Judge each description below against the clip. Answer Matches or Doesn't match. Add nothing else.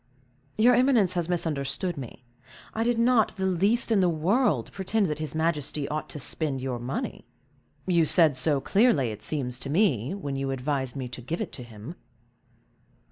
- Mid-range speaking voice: Matches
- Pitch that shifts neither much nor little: Doesn't match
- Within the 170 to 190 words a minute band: Matches